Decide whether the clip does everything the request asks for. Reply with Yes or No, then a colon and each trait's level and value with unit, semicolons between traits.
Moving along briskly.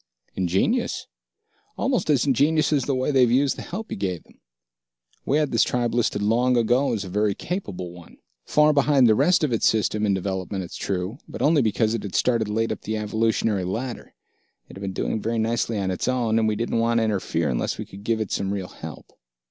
Yes: fast, 220 wpm